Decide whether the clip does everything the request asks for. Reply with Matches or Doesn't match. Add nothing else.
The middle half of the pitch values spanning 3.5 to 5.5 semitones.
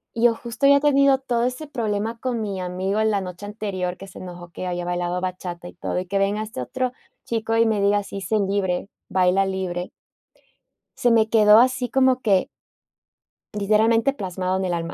Matches